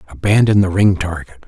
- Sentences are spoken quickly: No, average, 160 wpm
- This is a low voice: Yes, very low, 90 Hz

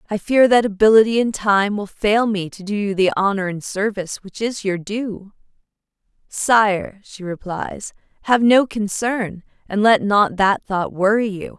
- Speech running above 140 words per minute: Yes, average, 170 wpm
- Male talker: No, female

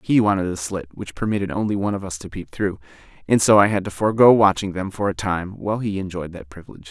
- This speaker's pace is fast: Yes, fast, 250 wpm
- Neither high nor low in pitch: No, very low, 95 Hz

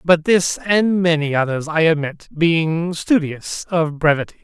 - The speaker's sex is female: No, male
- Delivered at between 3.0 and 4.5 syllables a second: Yes, 4.0 syllables/s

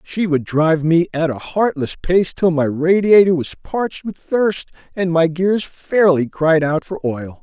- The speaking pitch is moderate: Yes, medium, 170 Hz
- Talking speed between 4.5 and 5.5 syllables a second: No, 4.2 syllables/s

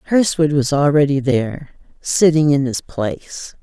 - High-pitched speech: No, medium, 145 Hz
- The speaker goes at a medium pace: No, slow, 130 wpm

